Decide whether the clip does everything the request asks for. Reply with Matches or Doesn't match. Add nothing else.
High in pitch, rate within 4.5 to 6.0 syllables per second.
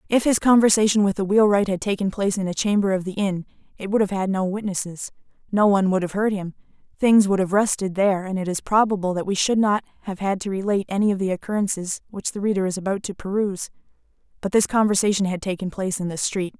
Doesn't match